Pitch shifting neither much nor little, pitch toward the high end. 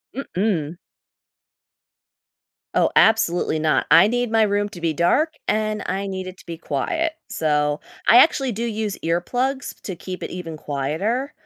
No: wide, 5.7 semitones; high, 195 Hz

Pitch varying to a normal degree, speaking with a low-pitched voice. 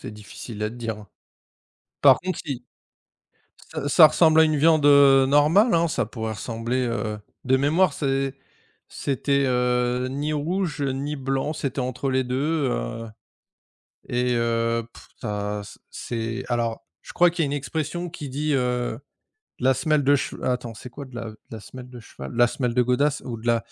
Yes: average, 3.7 semitones; low, 130 Hz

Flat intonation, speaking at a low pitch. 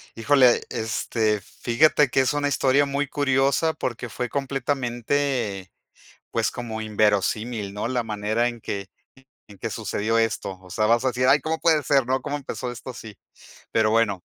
No: average, 4.0 semitones; low, 120 Hz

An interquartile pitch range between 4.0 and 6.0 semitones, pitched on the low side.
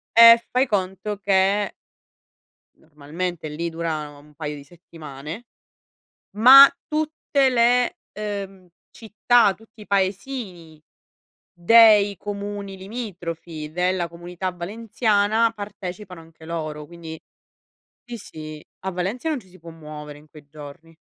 No: average, 4.7 semitones; medium, 185 Hz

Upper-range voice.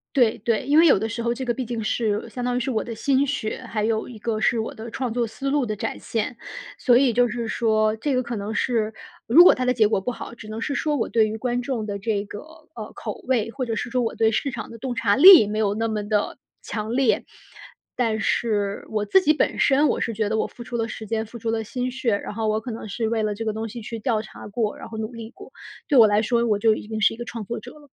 Yes: high, 225 Hz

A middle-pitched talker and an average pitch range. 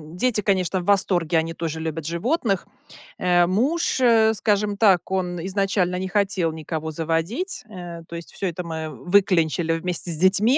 Yes: medium, 180 Hz; average, 3.5 semitones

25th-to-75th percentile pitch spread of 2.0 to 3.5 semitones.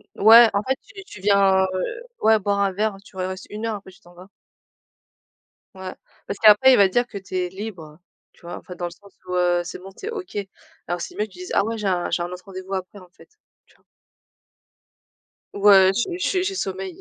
Yes: average, 2.8 semitones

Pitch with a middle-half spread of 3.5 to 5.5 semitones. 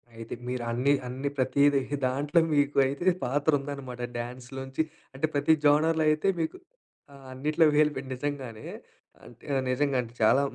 No: narrow, 2.5 semitones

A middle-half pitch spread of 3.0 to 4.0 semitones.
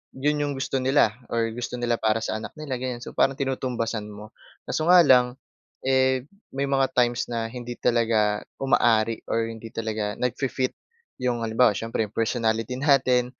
No: narrow, 2.6 semitones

